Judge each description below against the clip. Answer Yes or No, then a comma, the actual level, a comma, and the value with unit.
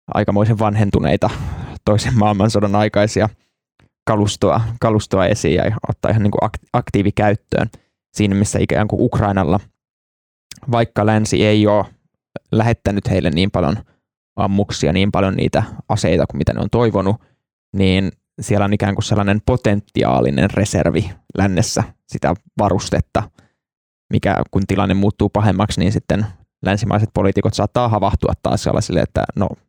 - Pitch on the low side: Yes, low, 105 Hz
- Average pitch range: No, narrow, 1.8 semitones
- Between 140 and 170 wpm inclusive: No, average, 125 wpm